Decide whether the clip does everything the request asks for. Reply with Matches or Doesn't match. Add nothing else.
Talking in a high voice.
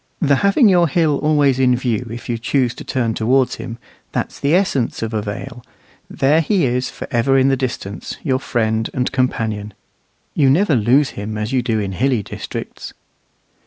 Doesn't match